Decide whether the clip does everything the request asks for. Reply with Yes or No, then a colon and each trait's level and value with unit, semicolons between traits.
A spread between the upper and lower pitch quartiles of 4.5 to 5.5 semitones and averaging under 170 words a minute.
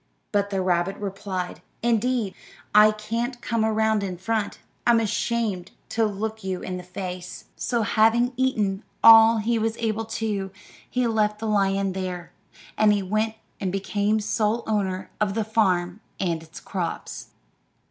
No: average, 2.7 semitones; average, 145 wpm